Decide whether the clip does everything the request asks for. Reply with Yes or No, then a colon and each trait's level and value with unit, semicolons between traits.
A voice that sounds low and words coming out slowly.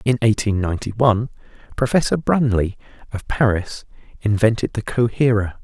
Yes: low, 110 Hz; slow, 115 wpm